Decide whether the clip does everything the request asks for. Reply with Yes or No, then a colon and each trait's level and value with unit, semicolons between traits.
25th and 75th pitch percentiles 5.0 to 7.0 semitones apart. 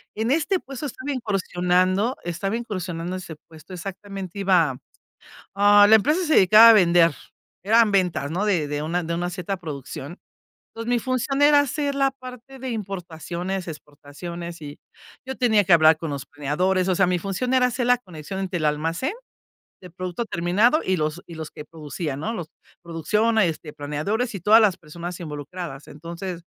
Yes: average, 5.3 semitones